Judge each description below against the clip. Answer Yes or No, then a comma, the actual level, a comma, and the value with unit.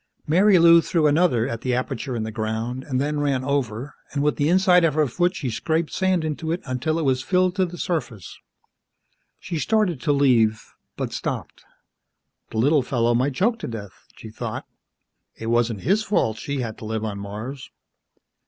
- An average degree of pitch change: No, wide, 6.1 semitones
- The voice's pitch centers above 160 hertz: No, medium, 140 Hz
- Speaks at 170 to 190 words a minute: Yes, average, 185 wpm